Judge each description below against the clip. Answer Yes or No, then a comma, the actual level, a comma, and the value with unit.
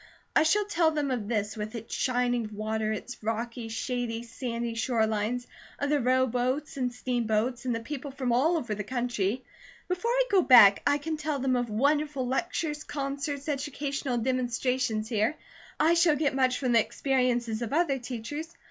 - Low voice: No, very high, 250 Hz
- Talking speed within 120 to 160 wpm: No, average, 175 wpm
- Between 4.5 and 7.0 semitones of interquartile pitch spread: No, average, 3.8 semitones